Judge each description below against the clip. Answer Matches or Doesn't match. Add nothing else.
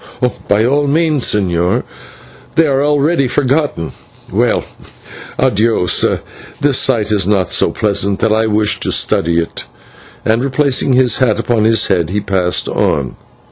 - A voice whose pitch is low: Matches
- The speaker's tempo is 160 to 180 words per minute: Doesn't match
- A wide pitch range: Matches